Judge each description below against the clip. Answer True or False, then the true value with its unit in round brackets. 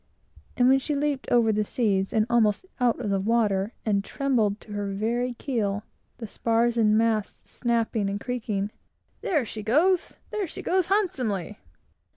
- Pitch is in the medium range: False (230 Hz)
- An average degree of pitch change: True (3.5 semitones)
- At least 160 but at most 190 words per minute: True (165 wpm)